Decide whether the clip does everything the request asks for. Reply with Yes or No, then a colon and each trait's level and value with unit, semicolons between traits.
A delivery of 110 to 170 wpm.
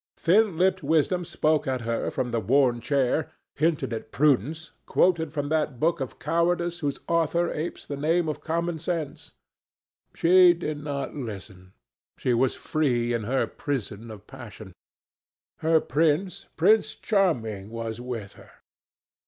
Yes: average, 145 wpm